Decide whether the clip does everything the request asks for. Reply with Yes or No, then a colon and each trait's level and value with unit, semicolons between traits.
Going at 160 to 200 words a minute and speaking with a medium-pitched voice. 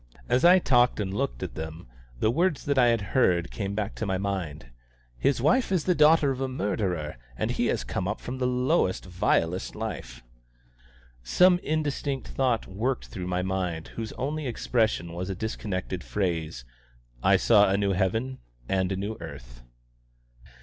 No: average, 170 wpm; low, 105 Hz